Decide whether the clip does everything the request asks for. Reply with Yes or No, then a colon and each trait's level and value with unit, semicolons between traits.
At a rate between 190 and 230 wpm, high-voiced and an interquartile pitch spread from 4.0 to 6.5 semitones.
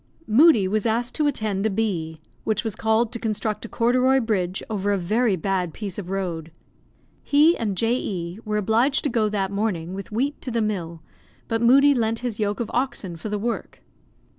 No: average, 195 wpm; high, 215 Hz; average, 3.5 semitones